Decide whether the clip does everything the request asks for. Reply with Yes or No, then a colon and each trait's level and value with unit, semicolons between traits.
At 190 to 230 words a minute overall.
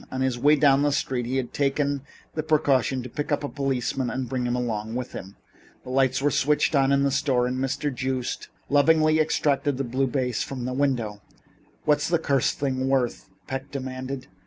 Yes: average, 200 wpm